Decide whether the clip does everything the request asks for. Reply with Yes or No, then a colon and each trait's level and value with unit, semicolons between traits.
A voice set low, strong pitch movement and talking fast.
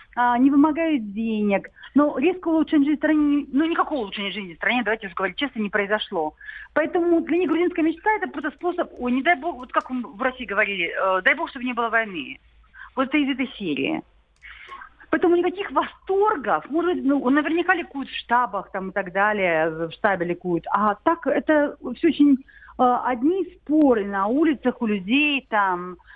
No: very high, 270 Hz; wide, 7.1 semitones; fast, 180 wpm